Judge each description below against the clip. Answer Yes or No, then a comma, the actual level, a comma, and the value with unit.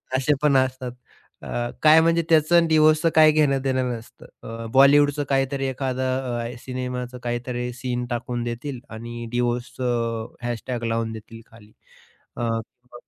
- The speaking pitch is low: Yes, low, 125 Hz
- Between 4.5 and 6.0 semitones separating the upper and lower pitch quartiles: No, narrow, 2.6 semitones